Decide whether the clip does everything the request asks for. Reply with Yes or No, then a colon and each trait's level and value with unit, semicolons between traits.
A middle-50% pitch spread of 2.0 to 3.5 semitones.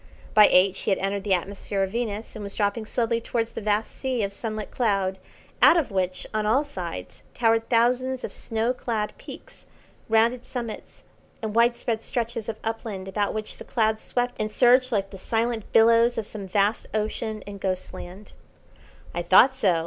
Yes: average, 2.7 semitones